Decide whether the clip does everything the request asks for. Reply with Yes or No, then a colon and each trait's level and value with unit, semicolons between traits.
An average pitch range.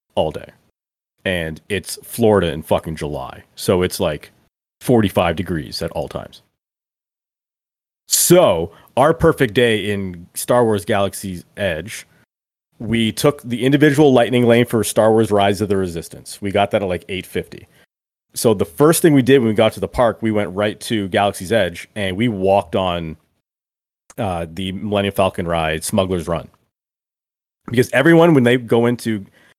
Yes: average, 4.1 semitones